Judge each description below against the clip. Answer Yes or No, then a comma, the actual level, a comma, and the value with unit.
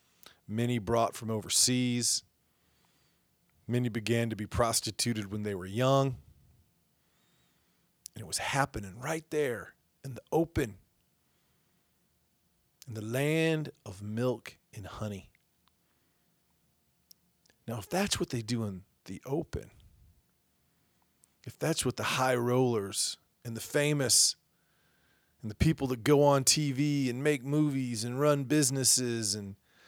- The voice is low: Yes, low, 120 Hz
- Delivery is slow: Yes, slow, 125 wpm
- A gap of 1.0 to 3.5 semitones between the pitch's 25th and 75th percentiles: No, average, 4.2 semitones